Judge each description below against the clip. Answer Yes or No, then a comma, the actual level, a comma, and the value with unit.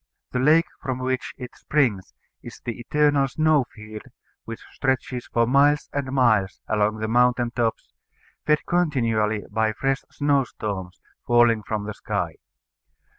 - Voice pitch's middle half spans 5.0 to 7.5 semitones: No, average, 4.0 semitones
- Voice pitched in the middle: No, low, 125 Hz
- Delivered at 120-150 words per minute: Yes, average, 140 wpm